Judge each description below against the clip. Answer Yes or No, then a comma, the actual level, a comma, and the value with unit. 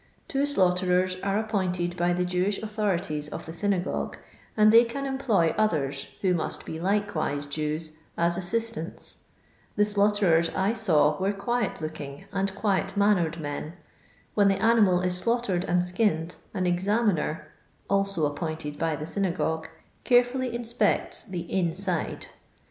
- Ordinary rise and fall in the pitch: Yes, average, 4.1 semitones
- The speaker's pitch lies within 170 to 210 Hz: Yes, medium, 185 Hz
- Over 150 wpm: No, average, 145 wpm